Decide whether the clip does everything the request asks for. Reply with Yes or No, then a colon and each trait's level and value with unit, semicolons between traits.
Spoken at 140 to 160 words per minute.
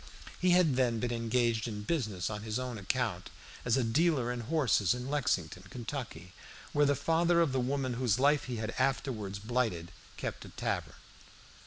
No: average, 175 wpm